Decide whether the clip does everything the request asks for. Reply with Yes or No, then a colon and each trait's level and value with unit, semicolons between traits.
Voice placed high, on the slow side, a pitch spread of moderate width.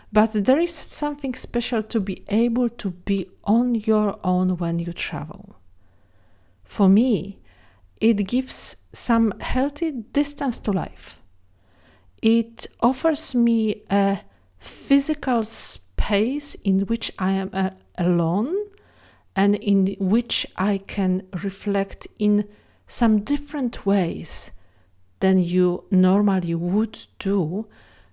Yes: high, 200 Hz; slow, 110 wpm; average, 4.9 semitones